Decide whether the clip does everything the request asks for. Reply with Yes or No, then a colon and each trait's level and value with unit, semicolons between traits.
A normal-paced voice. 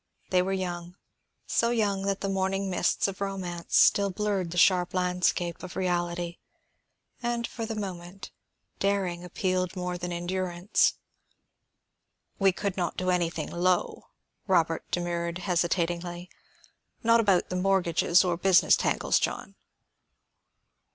No: slow, 125 wpm